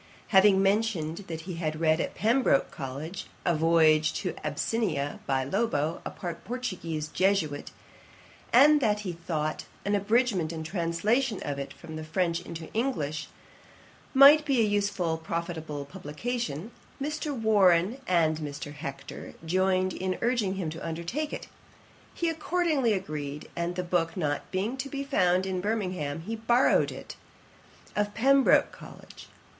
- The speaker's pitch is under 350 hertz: Yes, medium, 185 Hz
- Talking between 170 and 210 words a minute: No, average, 145 wpm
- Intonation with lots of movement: Yes, wide, 6.0 semitones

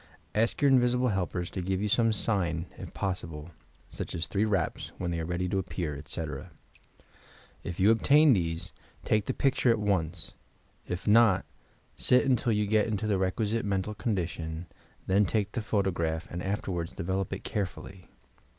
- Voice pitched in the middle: No, very low, 95 Hz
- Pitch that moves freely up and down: No, average, 3.8 semitones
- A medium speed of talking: Yes, average, 170 wpm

